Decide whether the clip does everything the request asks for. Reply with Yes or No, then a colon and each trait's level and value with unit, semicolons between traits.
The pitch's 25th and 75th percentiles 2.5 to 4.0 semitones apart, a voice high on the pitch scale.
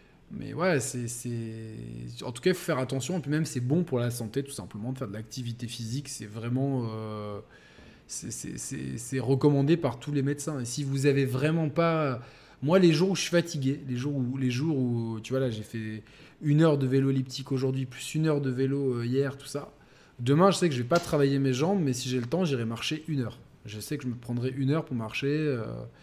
No: average, 3.4 semitones; low, 135 Hz